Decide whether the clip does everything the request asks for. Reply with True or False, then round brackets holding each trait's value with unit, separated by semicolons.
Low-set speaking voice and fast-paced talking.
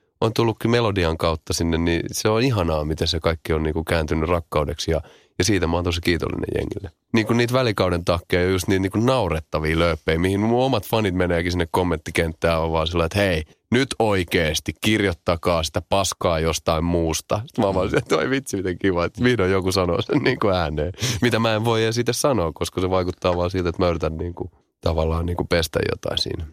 True (90 Hz; 205 wpm)